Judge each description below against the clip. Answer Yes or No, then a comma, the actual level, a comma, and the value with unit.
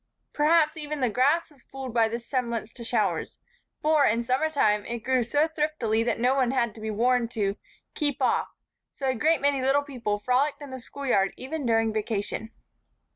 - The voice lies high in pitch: Yes, very high, 255 Hz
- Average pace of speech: Yes, average, 190 wpm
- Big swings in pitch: No, average, 4.1 semitones